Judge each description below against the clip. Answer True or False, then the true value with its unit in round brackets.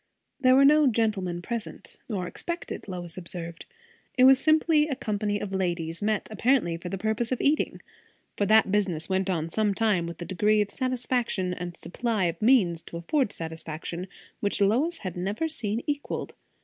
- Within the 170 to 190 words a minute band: True (180 wpm)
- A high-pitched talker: True (205 Hz)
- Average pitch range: False (5.8 semitones)